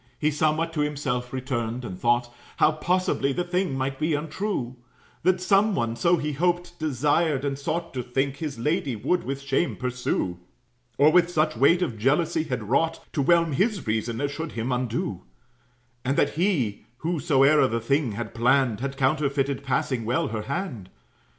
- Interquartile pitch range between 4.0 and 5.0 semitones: Yes, average, 4.7 semitones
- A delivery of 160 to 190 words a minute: Yes, average, 170 wpm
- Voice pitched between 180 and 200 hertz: No, medium, 140 Hz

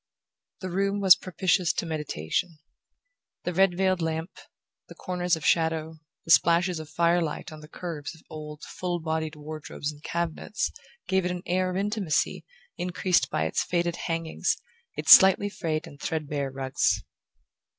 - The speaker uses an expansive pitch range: No, narrow, 2.6 semitones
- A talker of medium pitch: Yes, medium, 170 Hz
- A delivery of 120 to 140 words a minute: No, average, 150 wpm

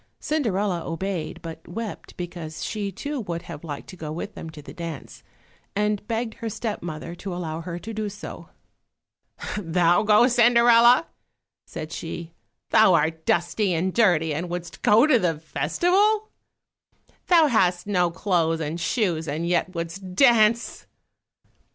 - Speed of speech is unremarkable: Yes, average, 150 wpm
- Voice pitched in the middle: Yes, medium, 180 Hz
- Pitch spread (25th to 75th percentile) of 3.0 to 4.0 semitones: No, average, 4.8 semitones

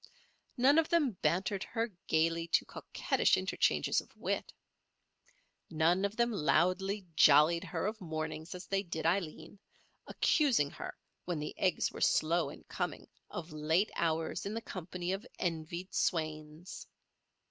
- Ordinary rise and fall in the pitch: Yes, average, 3.8 semitones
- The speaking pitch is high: No, medium, 175 Hz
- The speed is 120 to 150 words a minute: Yes, average, 140 wpm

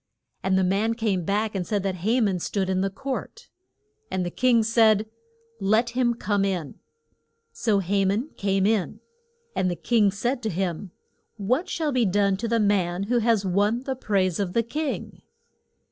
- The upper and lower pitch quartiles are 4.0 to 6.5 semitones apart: No, average, 3.3 semitones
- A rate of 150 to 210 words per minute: Yes, average, 180 wpm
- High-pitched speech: Yes, high, 205 Hz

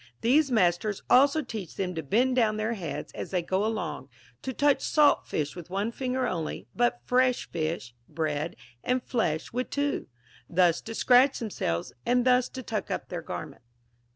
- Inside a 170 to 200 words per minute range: Yes, average, 175 wpm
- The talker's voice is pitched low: No, high, 215 Hz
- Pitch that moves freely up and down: Yes, wide, 6.9 semitones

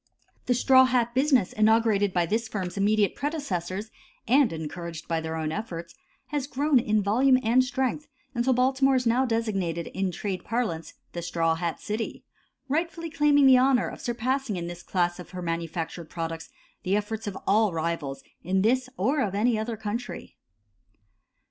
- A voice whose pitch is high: Yes, high, 215 Hz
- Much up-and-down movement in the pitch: Yes, wide, 6.6 semitones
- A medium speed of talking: Yes, average, 165 wpm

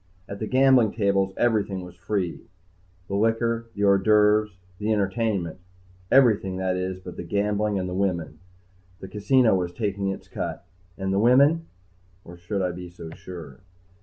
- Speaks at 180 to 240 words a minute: No, average, 165 wpm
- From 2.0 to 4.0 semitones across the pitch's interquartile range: Yes, average, 2.9 semitones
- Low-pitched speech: Yes, low, 100 Hz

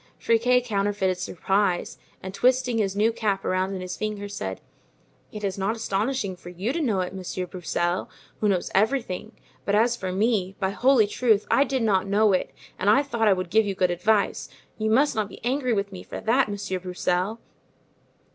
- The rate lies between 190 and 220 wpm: Yes, average, 195 wpm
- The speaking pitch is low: No, high, 205 Hz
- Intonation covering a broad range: No, average, 3.3 semitones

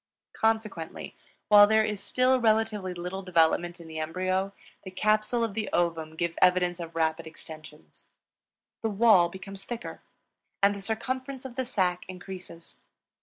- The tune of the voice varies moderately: Yes, average, 4.2 semitones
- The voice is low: No, high, 190 Hz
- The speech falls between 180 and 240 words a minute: No, average, 145 wpm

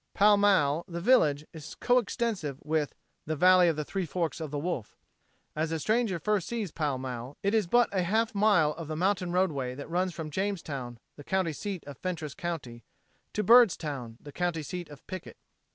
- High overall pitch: No, medium, 170 Hz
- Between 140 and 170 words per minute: No, average, 195 wpm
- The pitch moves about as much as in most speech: Yes, average, 4.8 semitones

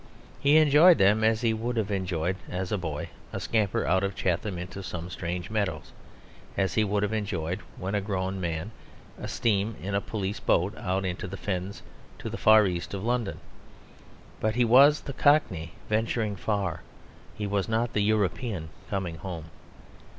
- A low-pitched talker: Yes, low, 100 Hz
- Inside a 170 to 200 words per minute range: Yes, average, 175 wpm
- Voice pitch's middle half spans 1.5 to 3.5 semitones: Yes, average, 3.2 semitones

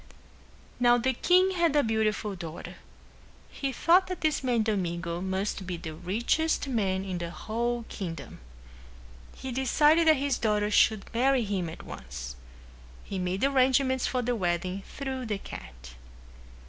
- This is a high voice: Yes, high, 220 Hz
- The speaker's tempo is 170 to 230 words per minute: No, average, 145 wpm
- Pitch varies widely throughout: Yes, wide, 6.3 semitones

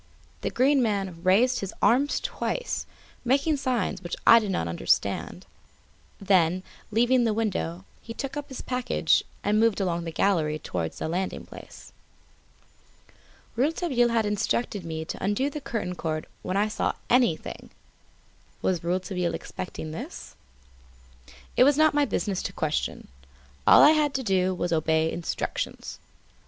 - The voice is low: No, high, 205 Hz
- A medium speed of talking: Yes, average, 145 wpm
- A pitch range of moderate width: No, wide, 6.6 semitones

